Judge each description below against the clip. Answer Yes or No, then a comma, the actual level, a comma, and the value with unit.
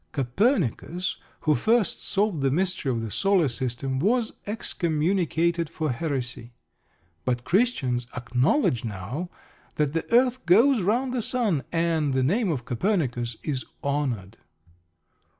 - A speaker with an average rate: No, slow, 125 wpm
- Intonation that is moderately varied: No, wide, 7.7 semitones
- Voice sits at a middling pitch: Yes, medium, 155 Hz